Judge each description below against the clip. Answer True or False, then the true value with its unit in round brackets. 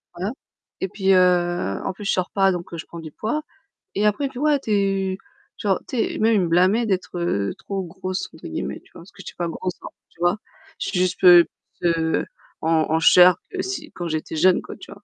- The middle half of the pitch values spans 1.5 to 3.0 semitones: True (2.7 semitones)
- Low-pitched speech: False (185 Hz)